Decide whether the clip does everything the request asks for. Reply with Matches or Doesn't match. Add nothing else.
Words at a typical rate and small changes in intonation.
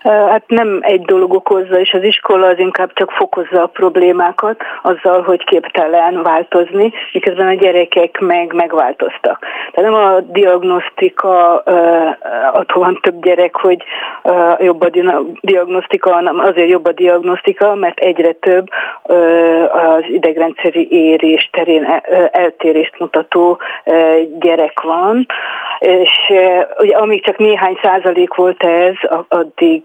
Matches